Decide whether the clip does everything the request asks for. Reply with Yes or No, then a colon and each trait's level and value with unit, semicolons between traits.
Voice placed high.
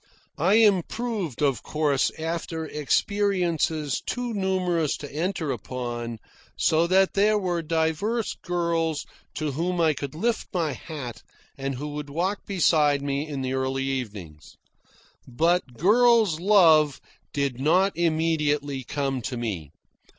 No: medium, 160 Hz